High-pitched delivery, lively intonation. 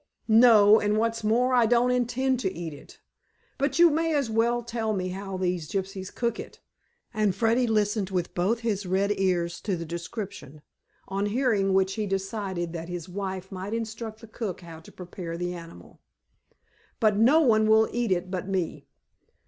No: high, 205 Hz; average, 3.8 semitones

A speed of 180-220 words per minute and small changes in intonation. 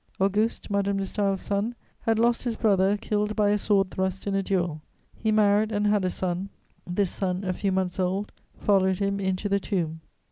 Yes: average, 200 wpm; narrow, 1.7 semitones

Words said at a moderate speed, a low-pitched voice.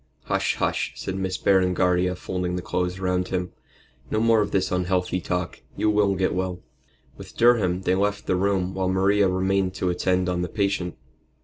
Yes: average, 180 wpm; very low, 95 Hz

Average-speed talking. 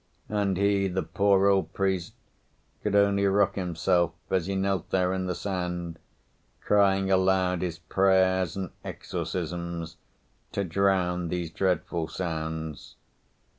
No: slow, 125 wpm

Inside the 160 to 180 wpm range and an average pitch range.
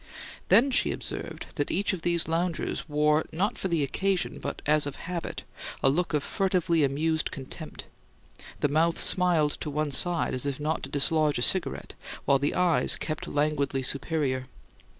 Yes: average, 170 wpm; average, 3.1 semitones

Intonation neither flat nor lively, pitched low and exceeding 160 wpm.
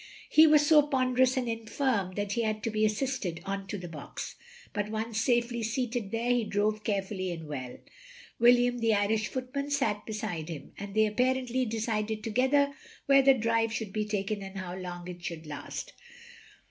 No: average, 3.9 semitones; high, 220 Hz; average, 180 wpm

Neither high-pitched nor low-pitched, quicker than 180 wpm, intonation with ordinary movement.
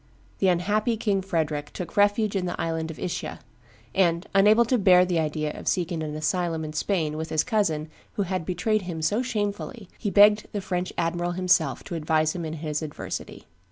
Yes: medium, 180 Hz; average, 190 wpm; average, 4.2 semitones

